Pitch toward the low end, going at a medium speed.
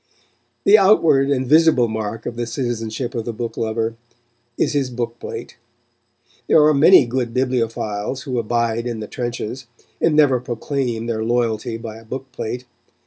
Yes: low, 120 Hz; average, 160 wpm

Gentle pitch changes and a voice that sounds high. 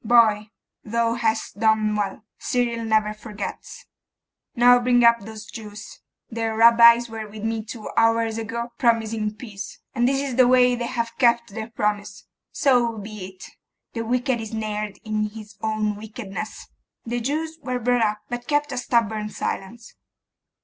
Yes: narrow, 2.1 semitones; high, 225 Hz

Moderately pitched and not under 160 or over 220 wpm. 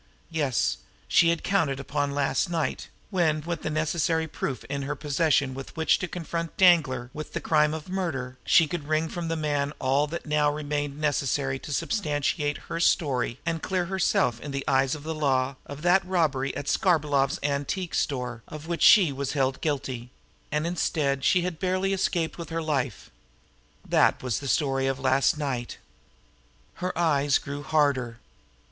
Yes: medium, 150 Hz; average, 175 wpm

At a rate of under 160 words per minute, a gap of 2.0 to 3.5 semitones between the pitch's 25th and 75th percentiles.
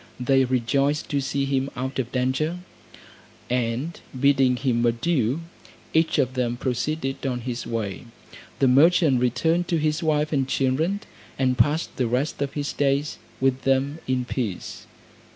Yes: average, 150 wpm; average, 2.9 semitones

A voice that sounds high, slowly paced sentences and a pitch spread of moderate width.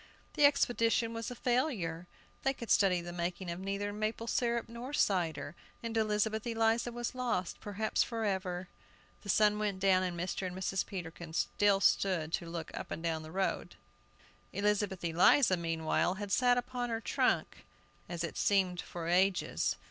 No: high, 195 Hz; average, 165 wpm; average, 4.5 semitones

